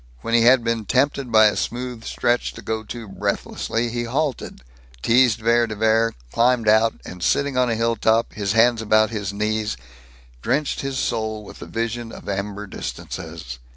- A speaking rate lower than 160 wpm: No, average, 175 wpm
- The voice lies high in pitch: No, low, 115 Hz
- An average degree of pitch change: No, narrow, 1.8 semitones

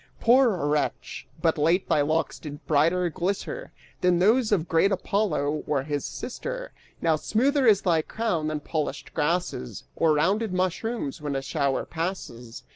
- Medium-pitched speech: Yes, medium, 165 Hz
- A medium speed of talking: Yes, average, 150 wpm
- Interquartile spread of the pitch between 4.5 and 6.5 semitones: Yes, average, 5.2 semitones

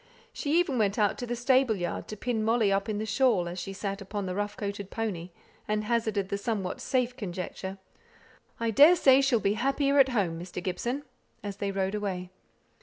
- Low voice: No, high, 210 Hz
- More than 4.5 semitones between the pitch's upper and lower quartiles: No, average, 3.8 semitones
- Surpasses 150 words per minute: Yes, average, 195 wpm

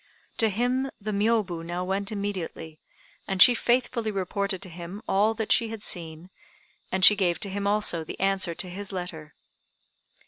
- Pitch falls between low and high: No, high, 195 Hz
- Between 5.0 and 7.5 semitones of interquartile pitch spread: No, average, 3.1 semitones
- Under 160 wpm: No, average, 170 wpm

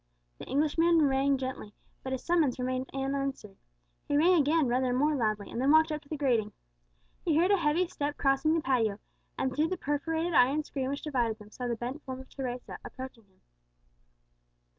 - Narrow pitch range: No, average, 3.4 semitones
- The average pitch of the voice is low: No, very high, 270 Hz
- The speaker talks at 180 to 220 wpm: Yes, average, 195 wpm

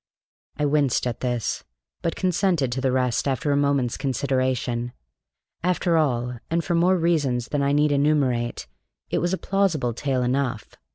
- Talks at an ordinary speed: Yes, average, 160 wpm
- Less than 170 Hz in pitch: Yes, medium, 140 Hz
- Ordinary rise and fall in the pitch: Yes, average, 4.2 semitones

